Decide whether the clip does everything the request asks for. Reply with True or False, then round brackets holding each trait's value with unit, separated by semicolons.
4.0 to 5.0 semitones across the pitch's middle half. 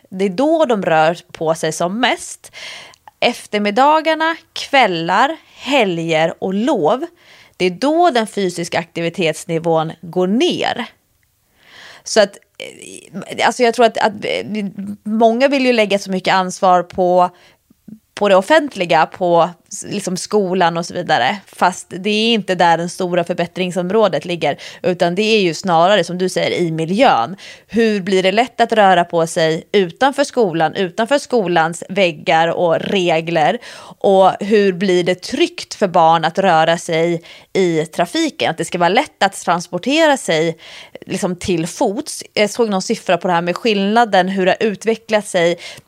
True (4.7 semitones)